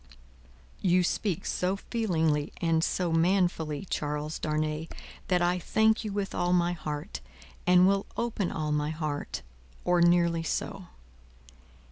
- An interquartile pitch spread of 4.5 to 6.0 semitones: No, average, 3.0 semitones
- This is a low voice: No, medium, 170 Hz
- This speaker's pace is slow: Yes, slow, 130 wpm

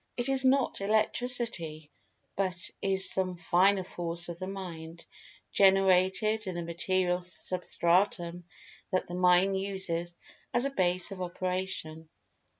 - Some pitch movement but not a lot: No, narrow, 2.2 semitones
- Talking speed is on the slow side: Yes, slow, 125 wpm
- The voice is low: No, medium, 185 Hz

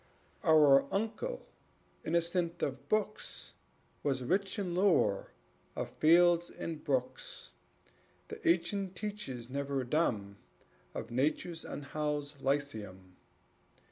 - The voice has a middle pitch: Yes, medium, 155 Hz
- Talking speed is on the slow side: Yes, slow, 95 wpm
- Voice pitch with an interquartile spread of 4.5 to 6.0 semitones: Yes, average, 4.8 semitones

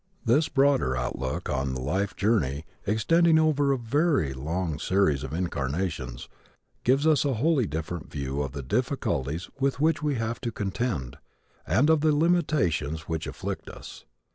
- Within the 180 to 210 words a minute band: No, average, 155 wpm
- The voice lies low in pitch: Yes, very low, 95 Hz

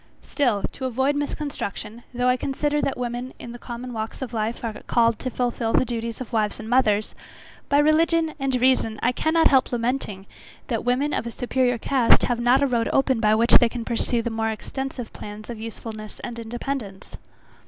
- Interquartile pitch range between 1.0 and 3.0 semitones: Yes, average, 2.7 semitones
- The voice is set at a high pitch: Yes, high, 240 Hz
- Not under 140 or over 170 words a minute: No, average, 190 wpm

